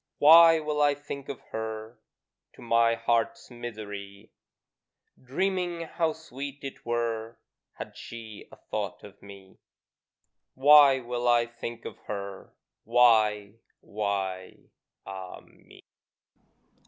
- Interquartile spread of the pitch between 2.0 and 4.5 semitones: No, average, 4.9 semitones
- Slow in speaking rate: Yes, slow, 110 wpm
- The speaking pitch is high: No, low, 120 Hz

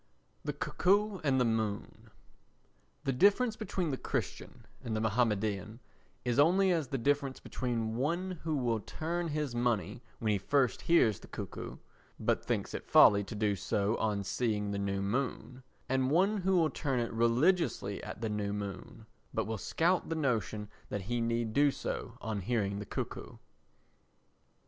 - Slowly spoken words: No, average, 165 wpm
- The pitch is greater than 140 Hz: No, low, 120 Hz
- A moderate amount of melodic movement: No, wide, 6.4 semitones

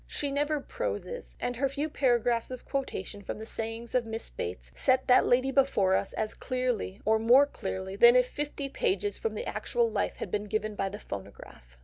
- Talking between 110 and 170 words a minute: No, average, 200 wpm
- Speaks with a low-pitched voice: No, high, 245 Hz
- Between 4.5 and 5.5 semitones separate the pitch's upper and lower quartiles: Yes, average, 4.8 semitones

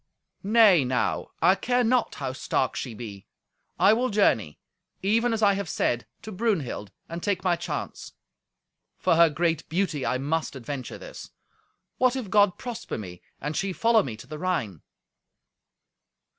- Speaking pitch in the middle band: Yes, medium, 175 Hz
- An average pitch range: No, wide, 8.4 semitones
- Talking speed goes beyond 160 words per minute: No, average, 155 wpm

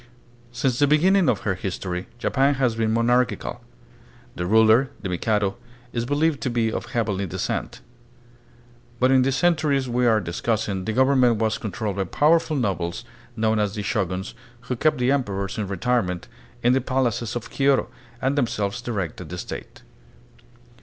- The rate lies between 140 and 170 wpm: Yes, average, 160 wpm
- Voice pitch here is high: No, low, 115 Hz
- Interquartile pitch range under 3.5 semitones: No, average, 4.6 semitones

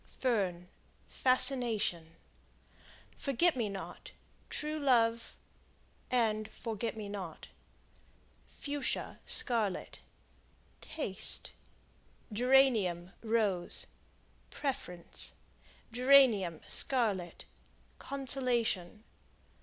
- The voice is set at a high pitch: Yes, high, 230 Hz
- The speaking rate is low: Yes, slow, 60 wpm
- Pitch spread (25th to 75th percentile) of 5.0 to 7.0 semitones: Yes, wide, 5.4 semitones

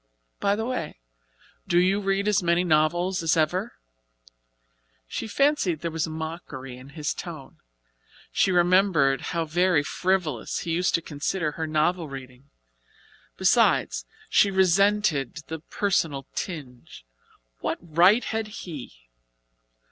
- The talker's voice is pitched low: No, medium, 170 Hz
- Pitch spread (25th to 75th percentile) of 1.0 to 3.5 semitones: No, average, 3.9 semitones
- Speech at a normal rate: No, slow, 125 wpm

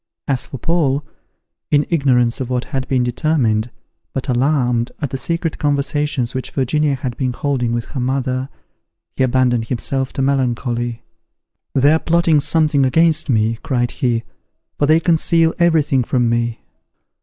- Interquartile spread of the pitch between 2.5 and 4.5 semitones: Yes, average, 3.4 semitones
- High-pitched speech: No, low, 135 Hz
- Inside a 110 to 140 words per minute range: No, average, 155 wpm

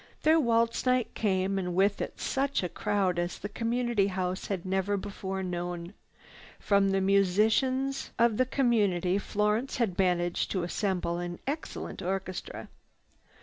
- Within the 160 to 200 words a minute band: No, average, 145 wpm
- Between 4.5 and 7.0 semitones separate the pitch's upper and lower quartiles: No, average, 4.0 semitones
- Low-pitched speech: No, high, 195 Hz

